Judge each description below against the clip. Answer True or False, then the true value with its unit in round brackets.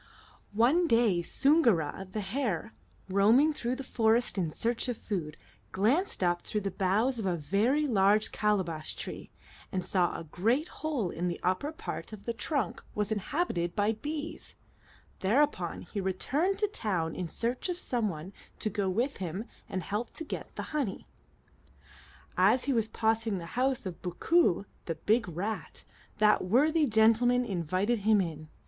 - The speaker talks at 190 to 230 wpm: False (165 wpm)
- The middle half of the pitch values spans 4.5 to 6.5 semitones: True (5.2 semitones)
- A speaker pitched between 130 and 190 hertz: False (215 Hz)